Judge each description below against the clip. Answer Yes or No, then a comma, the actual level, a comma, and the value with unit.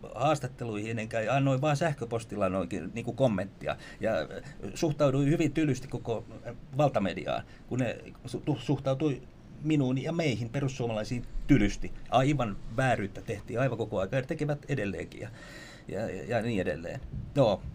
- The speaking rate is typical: Yes, average, 135 wpm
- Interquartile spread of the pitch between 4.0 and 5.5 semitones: Yes, average, 4.4 semitones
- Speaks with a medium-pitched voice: No, low, 130 Hz